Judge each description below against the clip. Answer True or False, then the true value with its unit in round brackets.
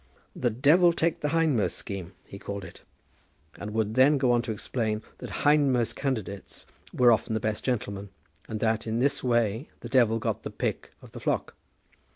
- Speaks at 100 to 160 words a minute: False (185 wpm)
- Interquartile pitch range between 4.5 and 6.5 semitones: False (3.7 semitones)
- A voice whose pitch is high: False (115 Hz)